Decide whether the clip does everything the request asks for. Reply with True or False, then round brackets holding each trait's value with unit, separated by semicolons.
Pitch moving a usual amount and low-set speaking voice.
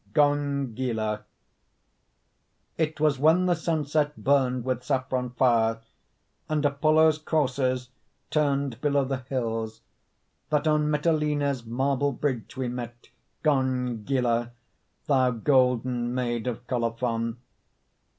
True (3.3 semitones; 130 Hz)